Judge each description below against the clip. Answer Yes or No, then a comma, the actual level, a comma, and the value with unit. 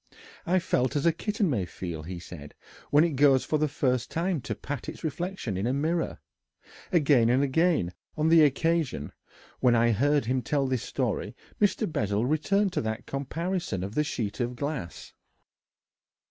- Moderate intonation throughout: No, wide, 5.7 semitones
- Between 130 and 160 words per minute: No, average, 175 wpm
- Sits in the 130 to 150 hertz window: Yes, medium, 140 Hz